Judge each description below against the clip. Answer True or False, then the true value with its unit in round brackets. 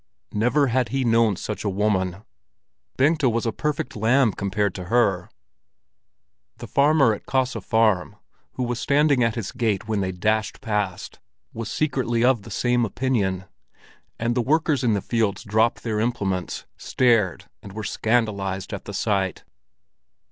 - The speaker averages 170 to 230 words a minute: False (155 wpm)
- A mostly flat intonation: False (3.6 semitones)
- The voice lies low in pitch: True (110 Hz)